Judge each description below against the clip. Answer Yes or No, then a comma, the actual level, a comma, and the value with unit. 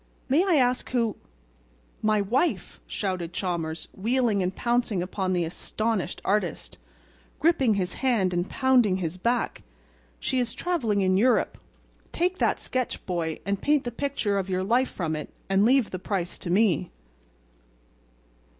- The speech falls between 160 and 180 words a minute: No, average, 150 wpm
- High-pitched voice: Yes, high, 210 Hz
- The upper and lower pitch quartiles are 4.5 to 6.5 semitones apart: Yes, average, 5.3 semitones